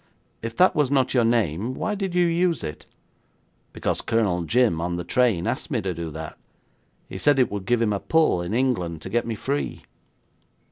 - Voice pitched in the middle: No, low, 115 Hz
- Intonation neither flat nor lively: No, wide, 7.2 semitones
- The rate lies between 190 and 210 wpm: Yes, average, 200 wpm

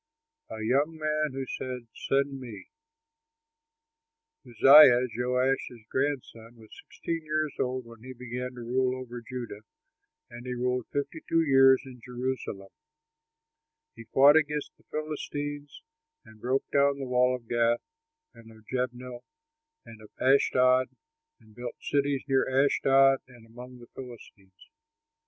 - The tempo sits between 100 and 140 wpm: Yes, slow, 135 wpm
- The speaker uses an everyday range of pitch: No, narrow, 2.3 semitones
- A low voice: Yes, low, 130 Hz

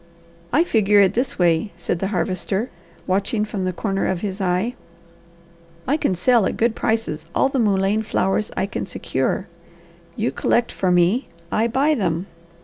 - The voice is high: Yes, high, 200 Hz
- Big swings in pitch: No, average, 3.5 semitones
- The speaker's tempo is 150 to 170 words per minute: Yes, average, 165 wpm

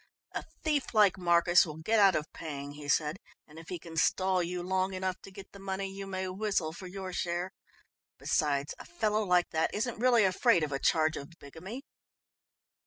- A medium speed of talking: Yes, average, 195 wpm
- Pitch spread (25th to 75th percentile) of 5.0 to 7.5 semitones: No, average, 3.2 semitones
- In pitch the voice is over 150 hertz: Yes, medium, 185 Hz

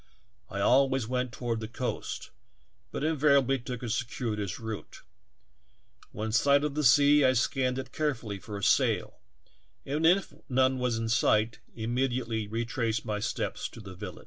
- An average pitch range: Yes, average, 3.3 semitones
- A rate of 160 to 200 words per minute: Yes, average, 165 wpm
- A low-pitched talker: Yes, low, 125 Hz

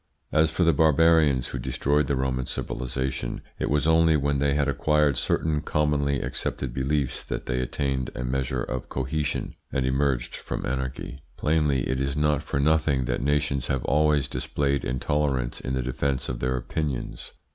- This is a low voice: Yes, very low, 70 Hz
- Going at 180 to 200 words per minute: No, average, 170 wpm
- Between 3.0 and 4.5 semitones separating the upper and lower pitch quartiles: No, narrow, 2.5 semitones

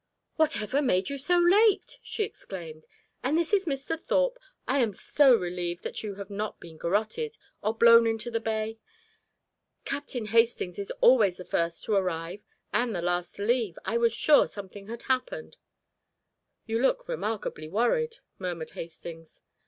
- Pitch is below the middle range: No, high, 225 Hz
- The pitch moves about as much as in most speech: No, wide, 7.1 semitones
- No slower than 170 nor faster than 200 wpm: No, average, 160 wpm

